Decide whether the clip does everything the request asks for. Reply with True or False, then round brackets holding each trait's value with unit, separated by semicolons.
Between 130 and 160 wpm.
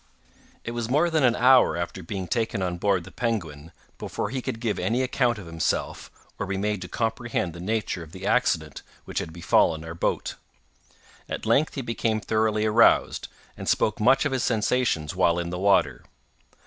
False (185 wpm)